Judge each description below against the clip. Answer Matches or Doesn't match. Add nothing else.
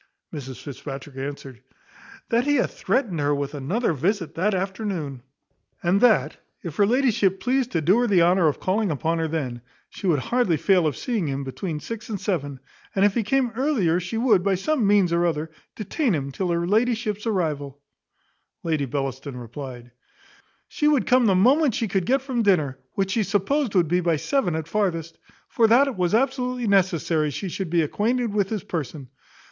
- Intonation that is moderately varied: Doesn't match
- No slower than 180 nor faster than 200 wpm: Matches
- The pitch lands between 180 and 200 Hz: Matches